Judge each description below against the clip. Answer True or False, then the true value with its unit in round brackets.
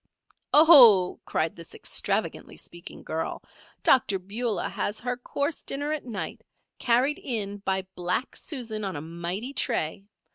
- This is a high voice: True (215 Hz)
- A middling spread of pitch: False (5.7 semitones)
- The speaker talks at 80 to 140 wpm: True (135 wpm)